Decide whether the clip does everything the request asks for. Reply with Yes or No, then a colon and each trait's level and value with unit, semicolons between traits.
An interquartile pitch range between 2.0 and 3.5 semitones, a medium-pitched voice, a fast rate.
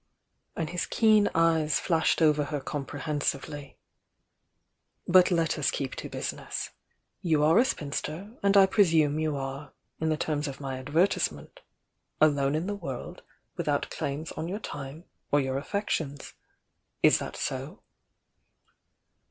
No: average, 3.1 semitones; medium, 155 Hz; average, 140 wpm